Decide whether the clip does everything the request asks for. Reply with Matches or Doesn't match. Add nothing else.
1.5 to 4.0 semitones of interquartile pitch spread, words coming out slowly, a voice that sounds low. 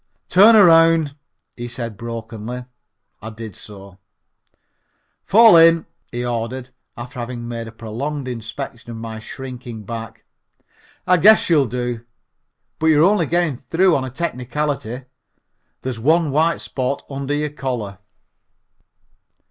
Doesn't match